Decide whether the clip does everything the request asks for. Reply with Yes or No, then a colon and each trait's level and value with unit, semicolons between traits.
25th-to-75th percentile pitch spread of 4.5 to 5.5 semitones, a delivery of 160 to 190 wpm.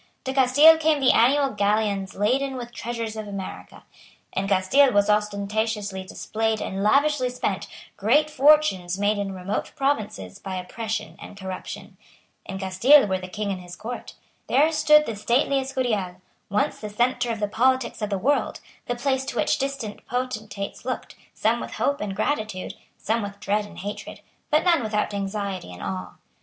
Yes: average, 4.8 semitones; average, 170 wpm